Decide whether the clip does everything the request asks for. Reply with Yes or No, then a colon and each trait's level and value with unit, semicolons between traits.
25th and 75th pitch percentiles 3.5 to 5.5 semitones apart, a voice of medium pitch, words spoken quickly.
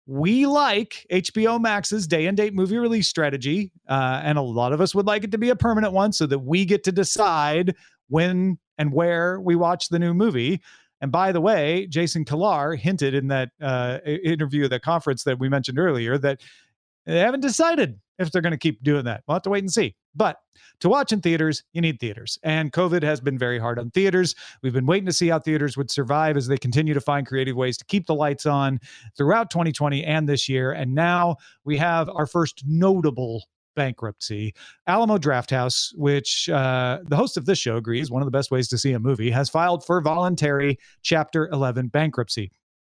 Yes: average, 5.0 semitones; medium, 150 Hz; fast, 210 wpm